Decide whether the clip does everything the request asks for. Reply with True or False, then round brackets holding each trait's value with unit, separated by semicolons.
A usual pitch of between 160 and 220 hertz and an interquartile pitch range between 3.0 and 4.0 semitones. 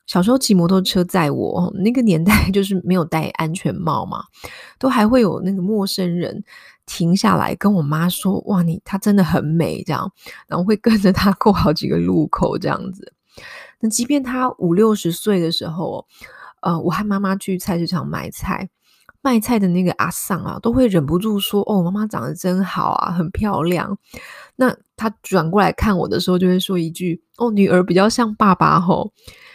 True (190 Hz; 3.4 semitones)